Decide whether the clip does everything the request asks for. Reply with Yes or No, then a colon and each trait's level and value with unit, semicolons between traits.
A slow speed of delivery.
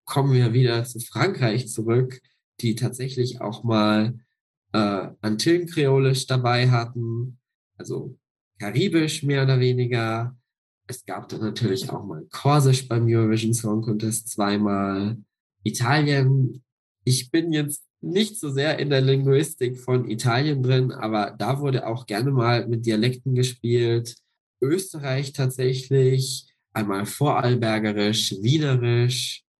Yes: slow, 120 wpm